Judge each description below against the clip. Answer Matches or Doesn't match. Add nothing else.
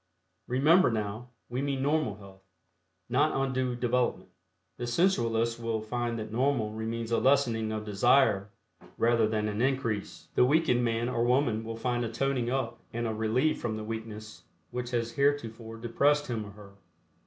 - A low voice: Matches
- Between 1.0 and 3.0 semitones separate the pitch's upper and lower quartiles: Matches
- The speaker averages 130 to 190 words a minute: Matches